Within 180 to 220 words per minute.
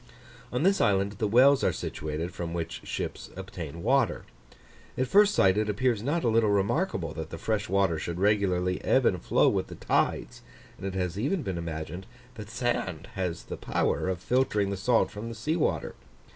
Yes: average, 190 wpm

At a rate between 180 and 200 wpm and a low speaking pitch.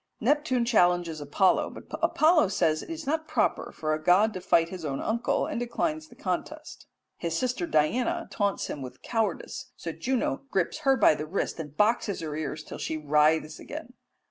No: average, 185 wpm; high, 190 Hz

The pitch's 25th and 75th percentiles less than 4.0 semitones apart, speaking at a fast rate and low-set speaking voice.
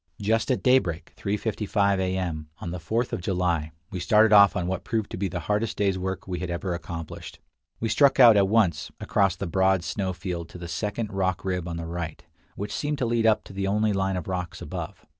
Yes: average, 3.2 semitones; fast, 225 wpm; very low, 95 Hz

